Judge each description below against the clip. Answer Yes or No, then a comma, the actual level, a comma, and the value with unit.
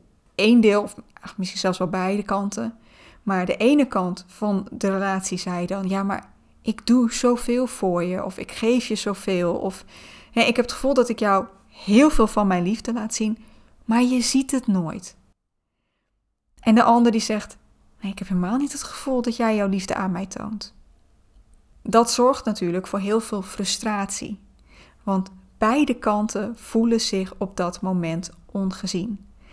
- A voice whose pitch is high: Yes, high, 210 Hz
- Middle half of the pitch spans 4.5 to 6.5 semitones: No, average, 3.3 semitones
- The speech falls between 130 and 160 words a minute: No, average, 175 wpm